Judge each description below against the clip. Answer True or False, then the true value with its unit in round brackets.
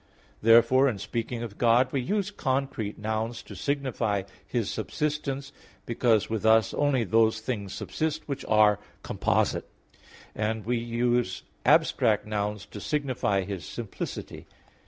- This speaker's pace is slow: True (130 wpm)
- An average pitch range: True (3.5 semitones)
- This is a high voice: False (115 Hz)